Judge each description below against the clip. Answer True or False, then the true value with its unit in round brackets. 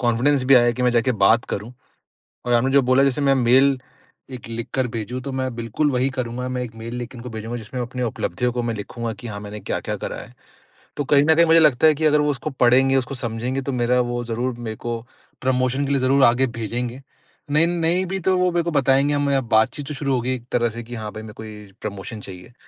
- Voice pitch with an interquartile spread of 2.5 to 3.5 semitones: True (2.8 semitones)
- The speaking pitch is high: False (125 Hz)